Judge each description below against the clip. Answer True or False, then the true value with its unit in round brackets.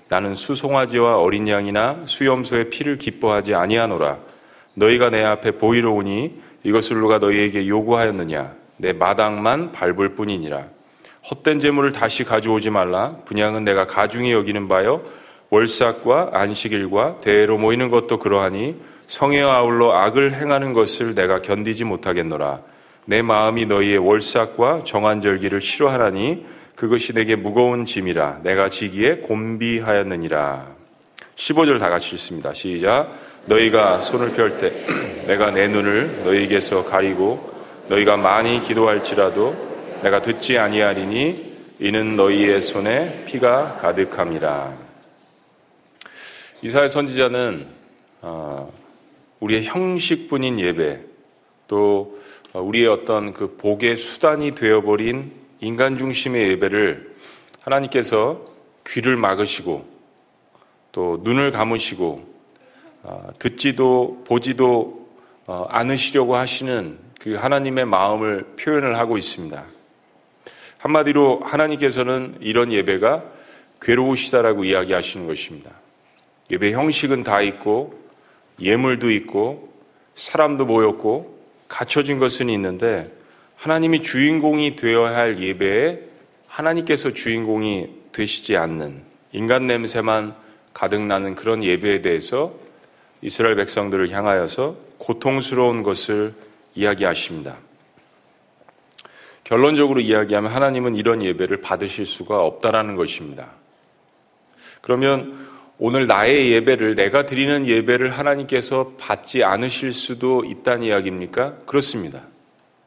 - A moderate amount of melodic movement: True (4.2 semitones)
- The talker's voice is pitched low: True (115 Hz)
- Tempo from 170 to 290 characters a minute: True (285 characters per minute)